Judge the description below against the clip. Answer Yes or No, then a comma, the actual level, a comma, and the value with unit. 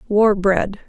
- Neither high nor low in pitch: No, high, 200 Hz